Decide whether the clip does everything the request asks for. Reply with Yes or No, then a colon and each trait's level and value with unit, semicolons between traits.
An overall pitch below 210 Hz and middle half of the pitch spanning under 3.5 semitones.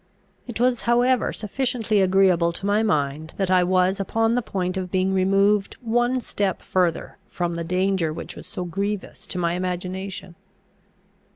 Yes: high, 190 Hz; average, 2.8 semitones